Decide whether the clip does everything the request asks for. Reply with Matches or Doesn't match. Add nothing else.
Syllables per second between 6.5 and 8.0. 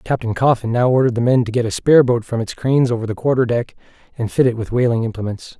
Matches